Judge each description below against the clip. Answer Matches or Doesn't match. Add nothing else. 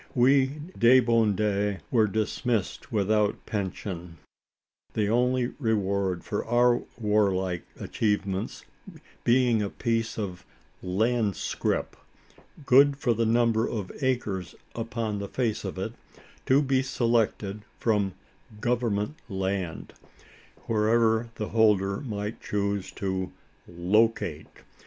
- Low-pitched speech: Matches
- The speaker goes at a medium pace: Doesn't match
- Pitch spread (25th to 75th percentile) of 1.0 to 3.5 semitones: Matches